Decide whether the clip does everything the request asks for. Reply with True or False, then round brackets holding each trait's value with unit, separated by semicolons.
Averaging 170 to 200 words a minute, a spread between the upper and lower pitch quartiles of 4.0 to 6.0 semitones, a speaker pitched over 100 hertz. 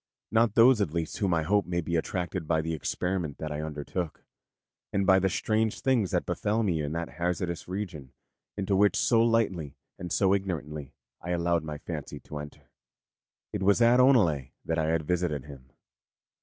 False (185 wpm; 4.3 semitones; 90 Hz)